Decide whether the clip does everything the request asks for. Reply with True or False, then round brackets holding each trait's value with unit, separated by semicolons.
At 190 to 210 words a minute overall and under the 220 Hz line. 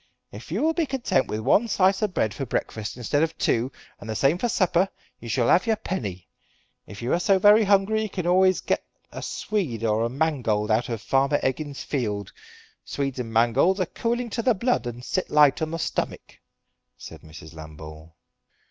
True (200 wpm; 140 Hz)